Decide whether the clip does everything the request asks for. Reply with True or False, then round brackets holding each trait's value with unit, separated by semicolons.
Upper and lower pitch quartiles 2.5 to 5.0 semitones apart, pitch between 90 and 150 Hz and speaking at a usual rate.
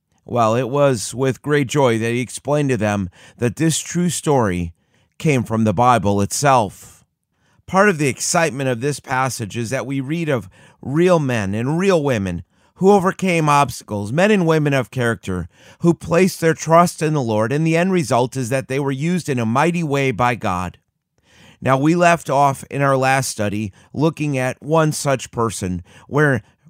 False (5.5 semitones; 135 Hz; 180 wpm)